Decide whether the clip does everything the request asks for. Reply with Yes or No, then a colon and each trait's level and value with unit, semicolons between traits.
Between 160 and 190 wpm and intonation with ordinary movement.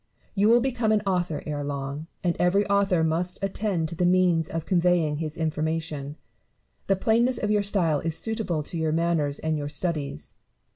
Yes: average, 180 wpm; average, 4.1 semitones